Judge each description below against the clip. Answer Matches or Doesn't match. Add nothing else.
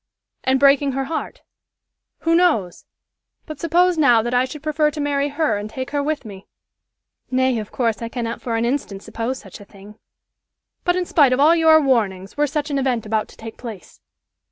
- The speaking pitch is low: Doesn't match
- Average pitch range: Matches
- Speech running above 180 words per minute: Matches